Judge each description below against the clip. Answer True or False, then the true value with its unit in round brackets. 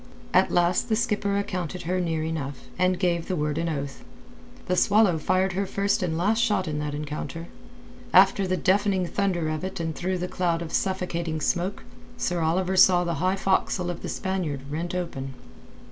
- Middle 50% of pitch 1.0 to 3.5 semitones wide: True (2.7 semitones)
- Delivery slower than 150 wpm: False (190 wpm)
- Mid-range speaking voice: True (180 Hz)